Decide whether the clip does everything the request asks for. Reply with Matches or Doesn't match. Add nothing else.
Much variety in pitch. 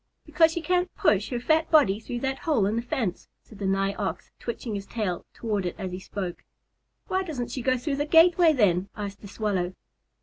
Matches